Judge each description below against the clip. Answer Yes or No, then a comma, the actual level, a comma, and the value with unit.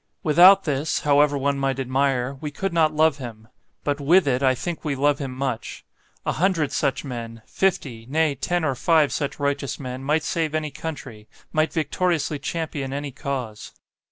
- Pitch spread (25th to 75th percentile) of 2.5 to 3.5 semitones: Yes, average, 2.9 semitones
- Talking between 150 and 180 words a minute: Yes, average, 175 wpm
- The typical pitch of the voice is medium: Yes, medium, 145 Hz